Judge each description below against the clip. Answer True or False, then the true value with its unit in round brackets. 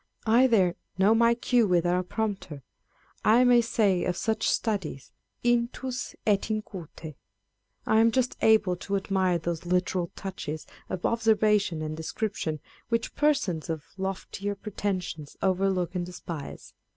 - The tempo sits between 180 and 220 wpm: False (140 wpm)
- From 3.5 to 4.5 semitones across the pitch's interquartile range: True (4.0 semitones)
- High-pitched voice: True (195 Hz)